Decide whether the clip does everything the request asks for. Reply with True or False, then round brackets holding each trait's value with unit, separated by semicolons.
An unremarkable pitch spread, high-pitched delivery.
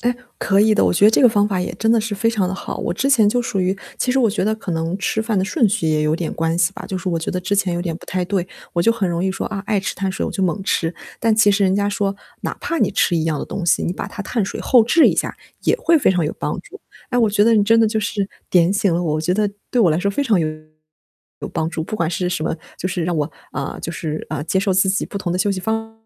True (3.8 semitones; 195 Hz)